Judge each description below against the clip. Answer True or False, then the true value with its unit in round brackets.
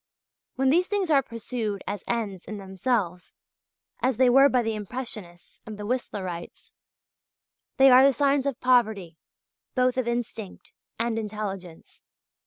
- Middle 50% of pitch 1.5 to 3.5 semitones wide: False (4.2 semitones)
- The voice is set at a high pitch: True (230 Hz)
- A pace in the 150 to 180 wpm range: False (140 wpm)